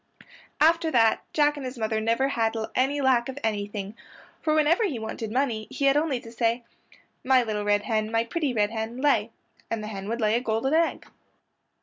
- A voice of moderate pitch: No, high, 235 Hz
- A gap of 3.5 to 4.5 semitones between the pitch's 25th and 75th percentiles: Yes, average, 4.0 semitones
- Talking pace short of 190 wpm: No, average, 200 wpm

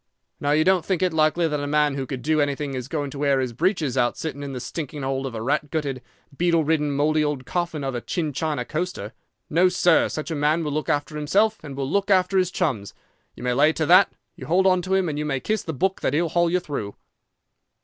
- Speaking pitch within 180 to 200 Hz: No, medium, 150 Hz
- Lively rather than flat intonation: No, average, 3.8 semitones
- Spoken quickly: Yes, fast, 250 wpm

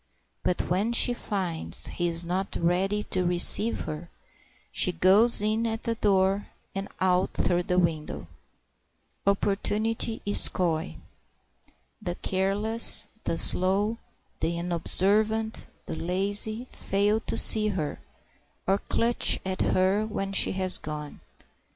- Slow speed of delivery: Yes, slow, 125 wpm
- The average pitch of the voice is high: Yes, high, 195 Hz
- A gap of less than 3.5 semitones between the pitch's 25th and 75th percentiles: Yes, average, 3.1 semitones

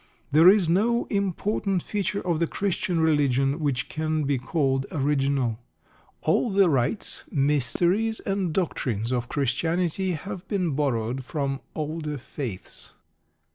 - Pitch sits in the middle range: Yes, medium, 155 Hz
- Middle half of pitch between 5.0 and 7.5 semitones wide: Yes, average, 5.3 semitones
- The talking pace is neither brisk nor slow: No, slow, 125 wpm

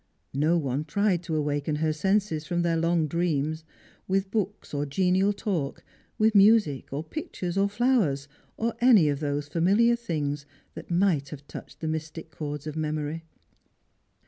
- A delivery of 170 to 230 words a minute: No, average, 155 wpm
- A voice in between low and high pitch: Yes, medium, 165 Hz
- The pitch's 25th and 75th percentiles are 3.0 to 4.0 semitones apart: No, average, 4.9 semitones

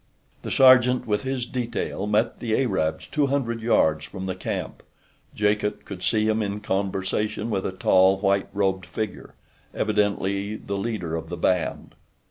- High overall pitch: No, low, 105 Hz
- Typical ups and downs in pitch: Yes, average, 3.0 semitones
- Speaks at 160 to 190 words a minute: No, average, 150 wpm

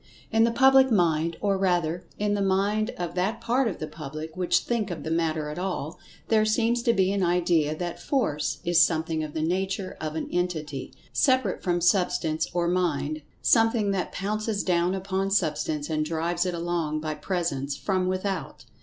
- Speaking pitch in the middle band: Yes, medium, 180 Hz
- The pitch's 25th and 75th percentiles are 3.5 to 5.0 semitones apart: Yes, average, 3.9 semitones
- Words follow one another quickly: No, average, 170 wpm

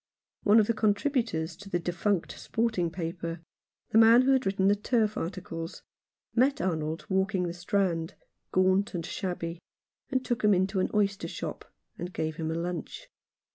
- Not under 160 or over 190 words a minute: Yes, average, 165 wpm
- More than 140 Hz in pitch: Yes, high, 190 Hz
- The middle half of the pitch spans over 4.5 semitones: No, average, 4.0 semitones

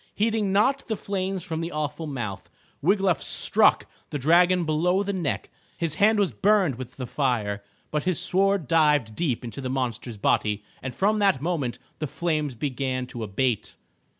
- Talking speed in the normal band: Yes, average, 170 wpm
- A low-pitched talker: No, medium, 155 Hz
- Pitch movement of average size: No, wide, 6.8 semitones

